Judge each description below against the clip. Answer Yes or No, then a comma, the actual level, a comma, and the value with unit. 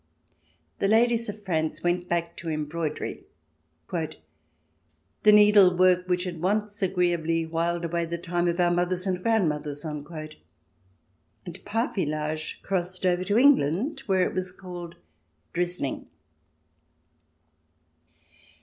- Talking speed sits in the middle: No, slow, 115 wpm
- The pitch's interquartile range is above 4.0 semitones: No, average, 3.4 semitones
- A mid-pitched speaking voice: Yes, medium, 175 Hz